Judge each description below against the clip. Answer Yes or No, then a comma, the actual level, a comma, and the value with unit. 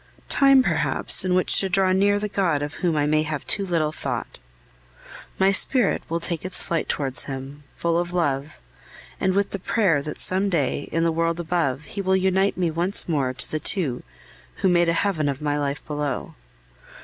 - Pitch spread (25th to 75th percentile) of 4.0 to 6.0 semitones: Yes, average, 4.3 semitones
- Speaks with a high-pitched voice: No, medium, 170 Hz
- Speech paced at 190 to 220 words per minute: Yes, average, 195 wpm